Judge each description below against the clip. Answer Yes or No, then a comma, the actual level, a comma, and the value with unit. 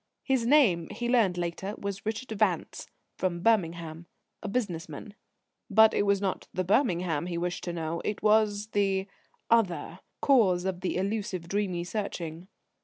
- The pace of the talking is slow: No, average, 155 wpm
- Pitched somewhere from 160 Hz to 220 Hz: Yes, high, 190 Hz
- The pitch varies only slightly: No, average, 3.6 semitones